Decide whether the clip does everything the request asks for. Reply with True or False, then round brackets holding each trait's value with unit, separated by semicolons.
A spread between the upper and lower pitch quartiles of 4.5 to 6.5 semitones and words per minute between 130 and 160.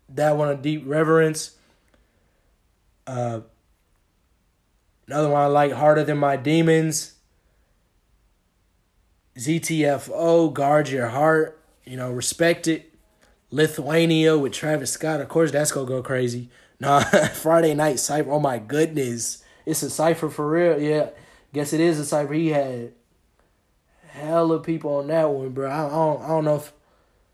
True (4.8 semitones; 145 wpm)